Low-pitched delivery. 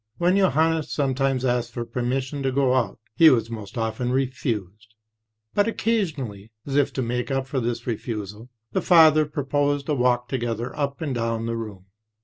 Yes: low, 130 Hz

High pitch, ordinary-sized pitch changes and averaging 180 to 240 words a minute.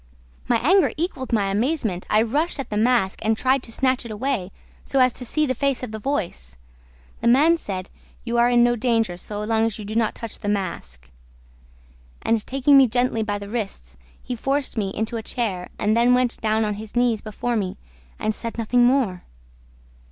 Yes: high, 230 Hz; average, 3.3 semitones; fast, 205 wpm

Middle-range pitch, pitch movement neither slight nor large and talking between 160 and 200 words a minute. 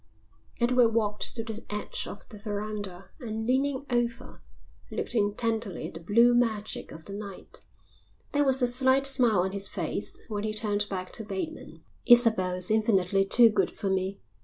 No: high, 215 Hz; average, 3.2 semitones; average, 170 wpm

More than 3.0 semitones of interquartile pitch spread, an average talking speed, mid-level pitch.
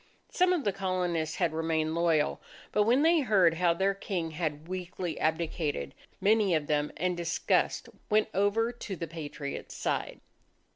Yes: average, 3.9 semitones; average, 155 wpm; medium, 175 Hz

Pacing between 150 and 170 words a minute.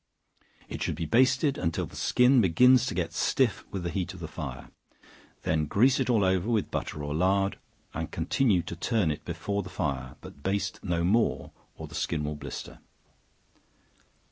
No: average, 180 wpm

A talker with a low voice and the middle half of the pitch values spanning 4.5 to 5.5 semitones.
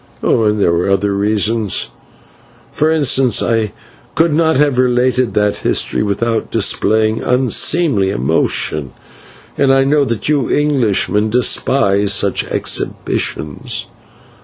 Yes: low, 115 Hz; average, 4.8 semitones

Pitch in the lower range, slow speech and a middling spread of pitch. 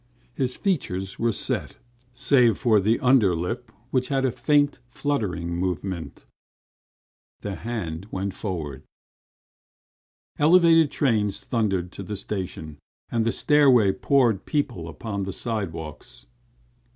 No: low, 105 Hz; slow, 120 wpm; wide, 5.7 semitones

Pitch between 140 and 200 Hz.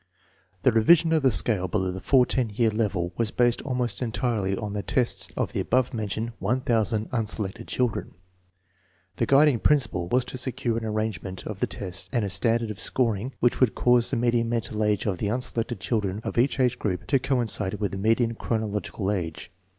No: low, 115 Hz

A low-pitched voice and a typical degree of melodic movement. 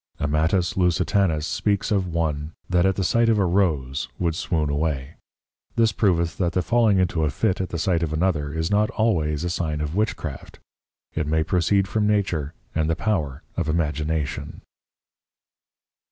Yes: very low, 85 Hz; average, 3.9 semitones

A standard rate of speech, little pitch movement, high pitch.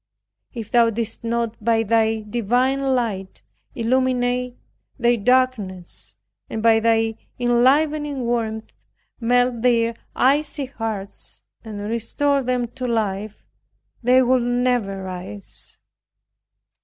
No: slow, 105 wpm; narrow, 2.2 semitones; high, 235 Hz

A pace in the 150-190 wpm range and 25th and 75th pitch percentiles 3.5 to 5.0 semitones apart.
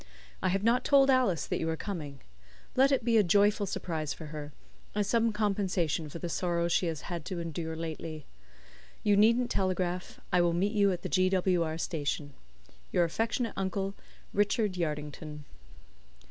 Yes: average, 175 wpm; average, 4.2 semitones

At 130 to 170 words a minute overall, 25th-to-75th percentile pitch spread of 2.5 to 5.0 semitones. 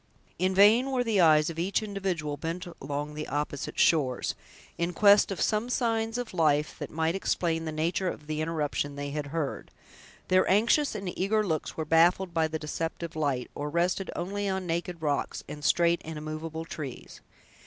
No: average, 180 wpm; average, 3.9 semitones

